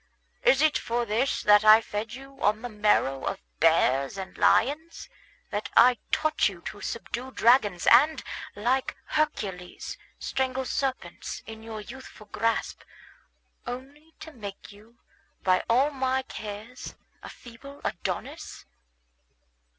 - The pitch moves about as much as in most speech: Yes, average, 4.2 semitones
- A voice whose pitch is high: Yes, high, 235 Hz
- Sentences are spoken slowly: Yes, slow, 125 wpm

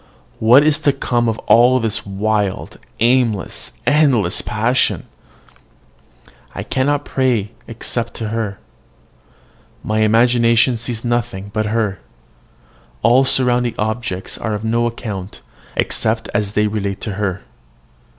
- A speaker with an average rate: No, slow, 120 wpm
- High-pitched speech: No, low, 115 Hz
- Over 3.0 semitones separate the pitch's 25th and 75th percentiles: No, narrow, 2.5 semitones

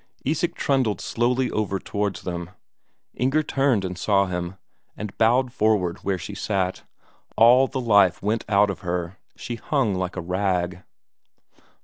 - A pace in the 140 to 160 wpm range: Yes, average, 145 wpm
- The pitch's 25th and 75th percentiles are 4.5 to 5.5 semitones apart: Yes, average, 4.8 semitones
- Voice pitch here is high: No, low, 100 Hz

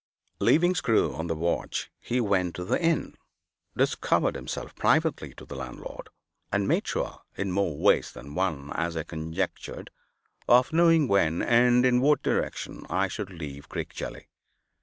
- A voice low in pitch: Yes, very low, 95 Hz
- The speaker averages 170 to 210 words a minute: No, average, 155 wpm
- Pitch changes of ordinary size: No, wide, 7.2 semitones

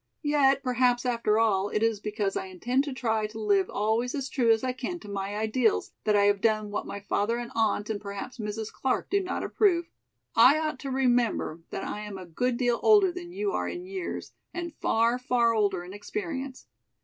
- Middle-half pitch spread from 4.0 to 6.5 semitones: Yes, average, 4.3 semitones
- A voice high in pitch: Yes, high, 235 Hz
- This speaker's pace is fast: Yes, fast, 210 wpm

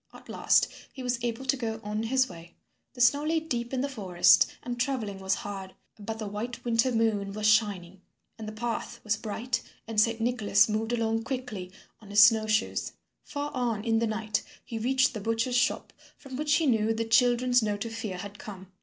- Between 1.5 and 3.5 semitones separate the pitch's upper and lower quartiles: Yes, average, 2.8 semitones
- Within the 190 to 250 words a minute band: Yes, fast, 205 wpm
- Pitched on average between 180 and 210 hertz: No, high, 225 Hz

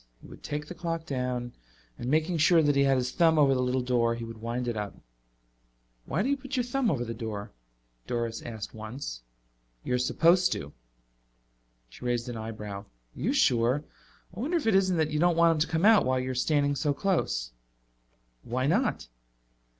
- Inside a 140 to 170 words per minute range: No, average, 195 wpm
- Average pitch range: No, wide, 6.1 semitones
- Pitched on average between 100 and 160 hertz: Yes, low, 135 Hz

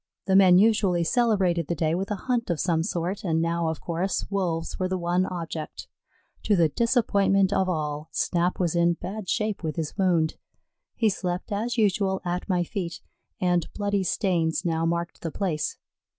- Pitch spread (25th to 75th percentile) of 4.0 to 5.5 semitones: No, average, 2.8 semitones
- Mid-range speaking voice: Yes, medium, 180 Hz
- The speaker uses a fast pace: No, average, 180 wpm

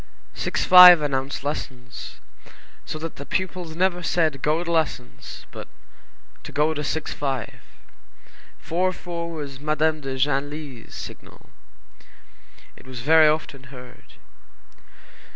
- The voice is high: No, medium, 150 Hz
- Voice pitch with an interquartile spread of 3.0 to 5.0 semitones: Yes, average, 3.4 semitones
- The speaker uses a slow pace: Yes, slow, 125 wpm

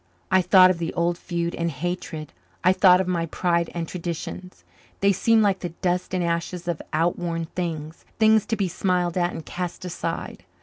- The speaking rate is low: No, average, 185 wpm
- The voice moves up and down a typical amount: No, narrow, 1.5 semitones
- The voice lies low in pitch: No, medium, 175 Hz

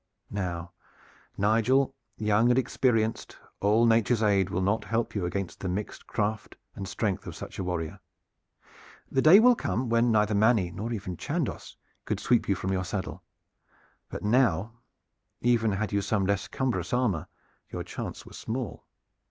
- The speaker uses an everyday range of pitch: Yes, average, 3.3 semitones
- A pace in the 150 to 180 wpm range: Yes, average, 160 wpm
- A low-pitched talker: Yes, low, 105 Hz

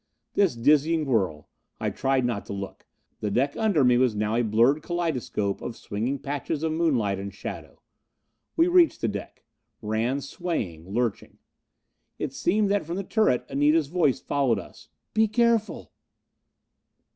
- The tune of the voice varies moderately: No, wide, 7.3 semitones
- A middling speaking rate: Yes, average, 150 wpm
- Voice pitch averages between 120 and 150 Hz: Yes, low, 135 Hz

